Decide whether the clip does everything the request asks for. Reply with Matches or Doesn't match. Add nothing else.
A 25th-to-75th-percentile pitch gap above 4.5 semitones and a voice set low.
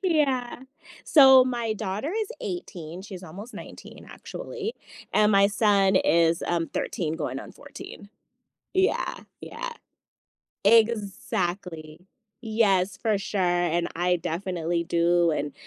Doesn't match